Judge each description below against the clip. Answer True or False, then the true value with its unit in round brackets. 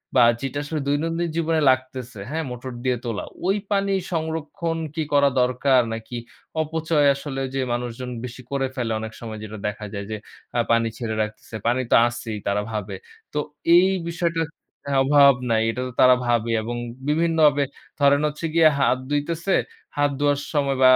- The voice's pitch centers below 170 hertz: True (135 Hz)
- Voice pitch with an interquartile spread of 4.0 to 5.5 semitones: True (4.5 semitones)